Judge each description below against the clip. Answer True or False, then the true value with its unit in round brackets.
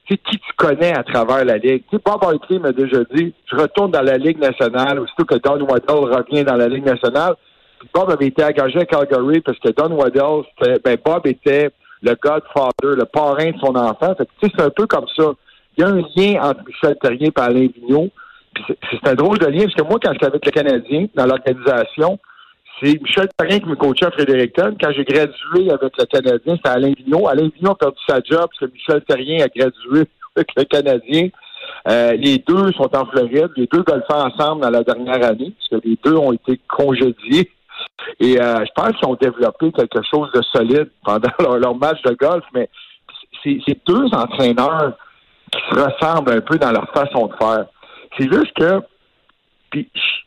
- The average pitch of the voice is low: False (150 Hz)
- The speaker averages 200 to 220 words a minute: True (210 wpm)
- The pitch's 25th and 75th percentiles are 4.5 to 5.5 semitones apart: True (4.8 semitones)